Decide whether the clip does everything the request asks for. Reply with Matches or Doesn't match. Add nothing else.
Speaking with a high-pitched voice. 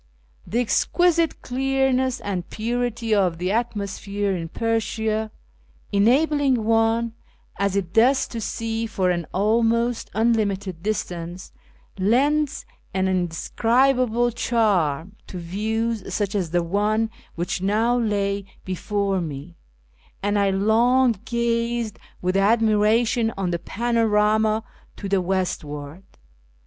Matches